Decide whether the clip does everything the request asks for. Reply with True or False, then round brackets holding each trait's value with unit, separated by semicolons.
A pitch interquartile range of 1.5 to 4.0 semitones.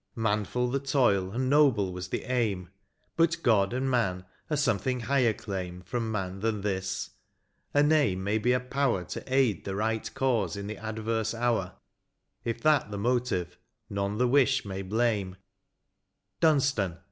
False (4.5 semitones)